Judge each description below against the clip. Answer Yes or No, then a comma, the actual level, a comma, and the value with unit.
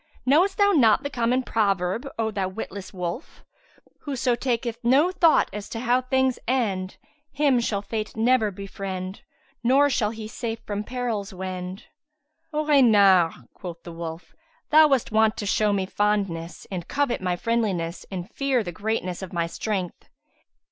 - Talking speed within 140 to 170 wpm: Yes, average, 155 wpm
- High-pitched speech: Yes, high, 215 Hz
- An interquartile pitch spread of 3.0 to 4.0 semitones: No, average, 5.1 semitones